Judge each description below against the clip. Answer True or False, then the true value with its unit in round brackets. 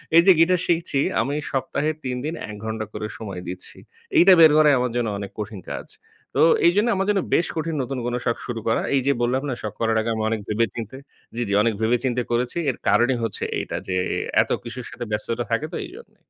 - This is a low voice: True (120 Hz)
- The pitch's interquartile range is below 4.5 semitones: False (5.3 semitones)